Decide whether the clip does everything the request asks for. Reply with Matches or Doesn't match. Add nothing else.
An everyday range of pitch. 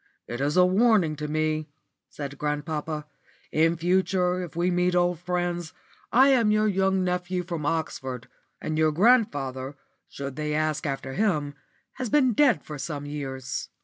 Matches